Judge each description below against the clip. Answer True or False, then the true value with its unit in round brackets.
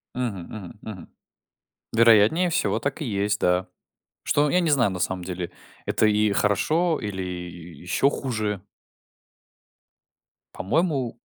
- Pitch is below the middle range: True (105 Hz)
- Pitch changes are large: True (6.7 semitones)